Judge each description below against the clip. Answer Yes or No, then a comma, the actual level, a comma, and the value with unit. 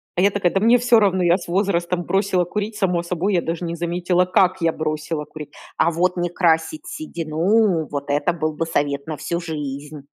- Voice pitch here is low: No, medium, 175 Hz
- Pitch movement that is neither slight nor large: Yes, average, 3.0 semitones